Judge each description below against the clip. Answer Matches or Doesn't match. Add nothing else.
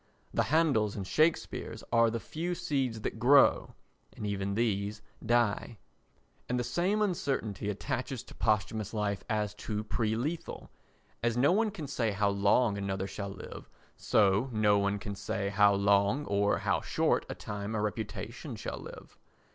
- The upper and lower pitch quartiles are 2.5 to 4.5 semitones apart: Matches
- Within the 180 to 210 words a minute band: Doesn't match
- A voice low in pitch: Matches